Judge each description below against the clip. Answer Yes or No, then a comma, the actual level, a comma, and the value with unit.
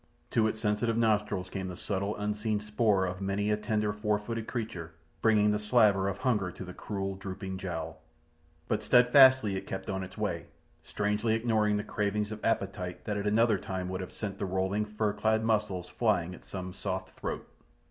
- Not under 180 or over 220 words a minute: Yes, average, 190 wpm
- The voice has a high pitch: No, low, 105 Hz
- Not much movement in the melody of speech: Yes, narrow, 2.2 semitones